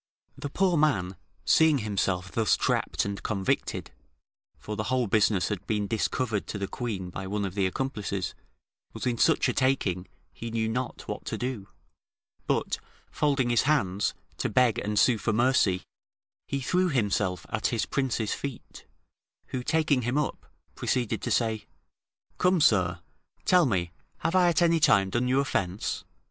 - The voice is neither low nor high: No, low, 115 Hz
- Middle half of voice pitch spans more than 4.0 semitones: Yes, average, 5.1 semitones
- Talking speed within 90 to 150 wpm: No, average, 160 wpm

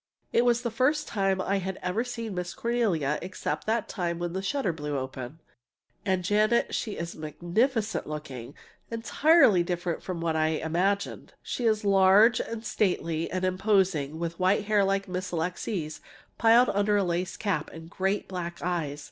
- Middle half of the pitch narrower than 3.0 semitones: No, average, 4.1 semitones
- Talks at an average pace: Yes, average, 170 wpm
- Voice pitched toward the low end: No, high, 190 Hz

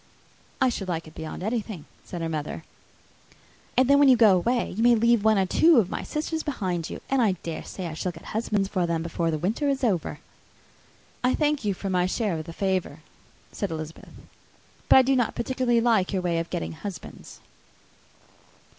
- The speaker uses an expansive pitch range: Yes, wide, 6.0 semitones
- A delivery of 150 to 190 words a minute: No, average, 200 wpm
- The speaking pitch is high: Yes, high, 195 Hz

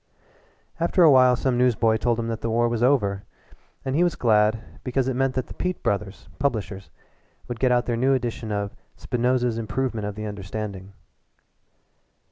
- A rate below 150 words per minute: No, average, 170 wpm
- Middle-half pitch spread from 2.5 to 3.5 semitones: Yes, average, 3.2 semitones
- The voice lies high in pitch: No, low, 120 Hz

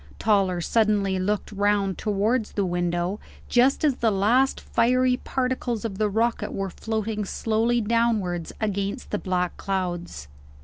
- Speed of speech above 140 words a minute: No, slow, 135 wpm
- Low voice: No, high, 210 Hz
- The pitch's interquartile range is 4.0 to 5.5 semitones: No, average, 3.4 semitones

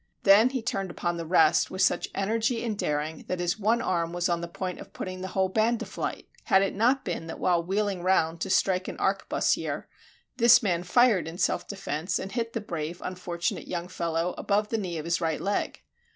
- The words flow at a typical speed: No, fast, 215 wpm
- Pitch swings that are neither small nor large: Yes, average, 3.6 semitones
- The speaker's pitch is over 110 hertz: Yes, medium, 185 Hz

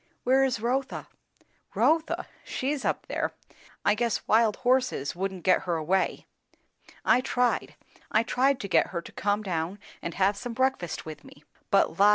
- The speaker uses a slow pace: No, average, 165 wpm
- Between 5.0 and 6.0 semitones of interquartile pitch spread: Yes, wide, 5.4 semitones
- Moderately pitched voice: No, high, 210 Hz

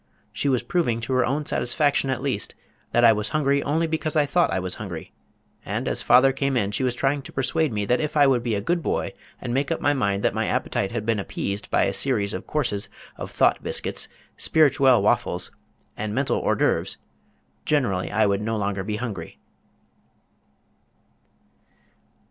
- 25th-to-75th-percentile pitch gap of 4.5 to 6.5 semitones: Yes, average, 5.3 semitones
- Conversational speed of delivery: Yes, average, 190 wpm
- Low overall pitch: Yes, low, 125 Hz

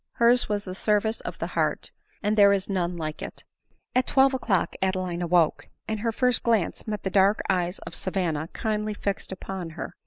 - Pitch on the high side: Yes, high, 200 Hz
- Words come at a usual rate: Yes, average, 190 wpm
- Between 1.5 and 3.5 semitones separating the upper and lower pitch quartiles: Yes, average, 3.2 semitones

